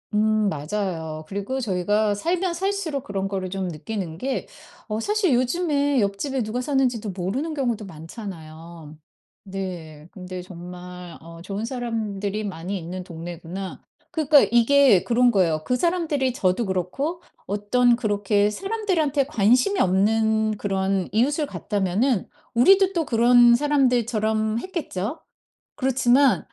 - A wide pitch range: Yes, wide, 6.1 semitones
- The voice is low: No, high, 215 Hz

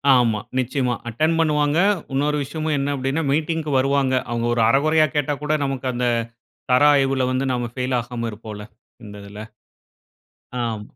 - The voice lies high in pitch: No, low, 135 Hz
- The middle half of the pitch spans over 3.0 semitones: Yes, average, 3.6 semitones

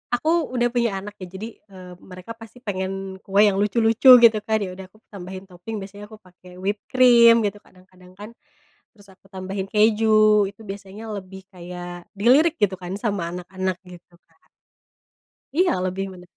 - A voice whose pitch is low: No, high, 195 Hz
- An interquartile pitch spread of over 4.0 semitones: No, average, 2.7 semitones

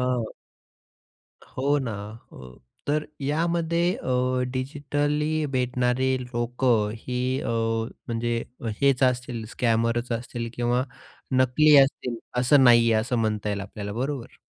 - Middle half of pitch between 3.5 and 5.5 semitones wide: No, average, 2.7 semitones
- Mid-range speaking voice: No, low, 125 Hz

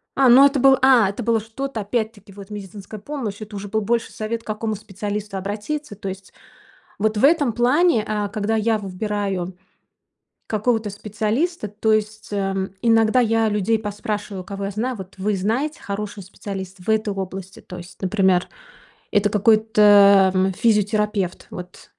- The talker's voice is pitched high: Yes, high, 210 Hz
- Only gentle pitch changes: Yes, narrow, 2.2 semitones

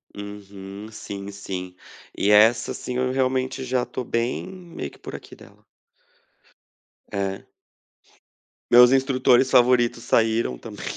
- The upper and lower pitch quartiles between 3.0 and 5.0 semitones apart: Yes, average, 4.1 semitones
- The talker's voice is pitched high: No, low, 115 Hz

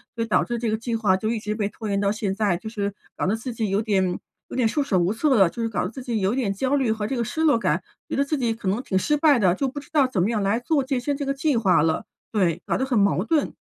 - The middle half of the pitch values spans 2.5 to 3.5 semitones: No, average, 4.7 semitones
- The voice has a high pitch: Yes, high, 225 Hz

